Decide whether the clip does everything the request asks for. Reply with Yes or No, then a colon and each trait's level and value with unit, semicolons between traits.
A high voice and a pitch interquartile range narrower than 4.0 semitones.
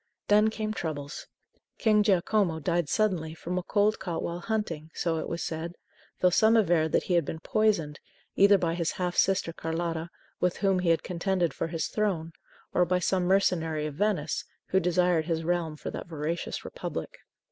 No: medium, 175 Hz; average, 3.2 semitones